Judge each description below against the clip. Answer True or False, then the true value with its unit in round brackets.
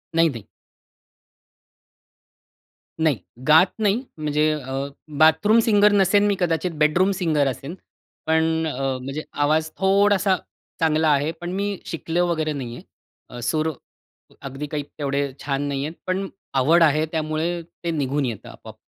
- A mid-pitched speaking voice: True (160 Hz)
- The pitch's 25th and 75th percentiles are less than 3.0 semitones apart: False (3.6 semitones)